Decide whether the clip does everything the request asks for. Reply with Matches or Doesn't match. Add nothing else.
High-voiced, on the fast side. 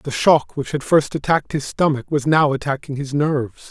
Doesn't match